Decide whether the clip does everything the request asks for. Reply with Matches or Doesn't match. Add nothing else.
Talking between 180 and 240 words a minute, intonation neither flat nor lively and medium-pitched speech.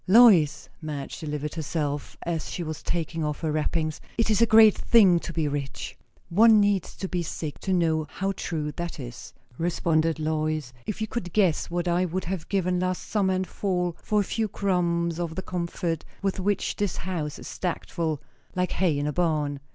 Matches